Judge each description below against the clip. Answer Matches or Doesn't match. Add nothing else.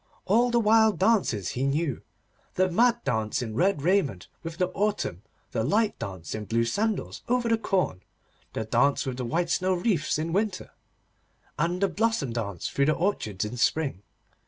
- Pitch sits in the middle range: Matches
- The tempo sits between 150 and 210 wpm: Matches